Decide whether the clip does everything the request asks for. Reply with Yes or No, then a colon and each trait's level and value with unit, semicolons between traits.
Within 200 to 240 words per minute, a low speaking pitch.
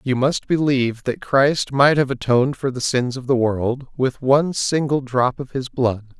Yes: fast, 205 wpm; low, 130 Hz